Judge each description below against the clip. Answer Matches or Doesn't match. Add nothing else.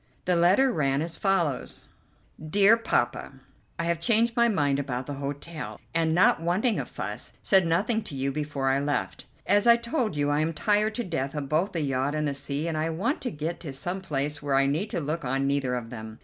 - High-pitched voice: Doesn't match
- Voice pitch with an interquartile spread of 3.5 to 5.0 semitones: Doesn't match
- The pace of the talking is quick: Matches